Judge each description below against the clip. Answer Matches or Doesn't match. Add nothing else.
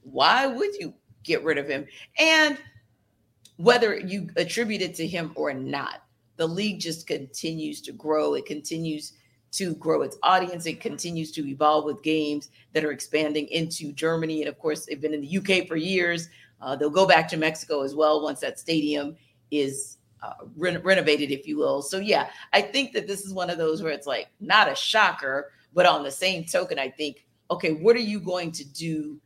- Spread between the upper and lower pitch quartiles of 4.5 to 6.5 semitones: Doesn't match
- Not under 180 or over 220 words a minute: Matches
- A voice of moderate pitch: Matches